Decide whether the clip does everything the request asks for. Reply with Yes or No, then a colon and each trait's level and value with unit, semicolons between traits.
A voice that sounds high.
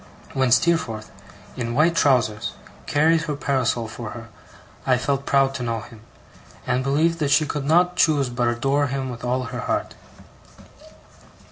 No: low, 135 Hz